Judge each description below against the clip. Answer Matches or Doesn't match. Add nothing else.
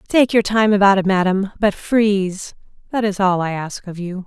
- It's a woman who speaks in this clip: Matches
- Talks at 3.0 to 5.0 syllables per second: Matches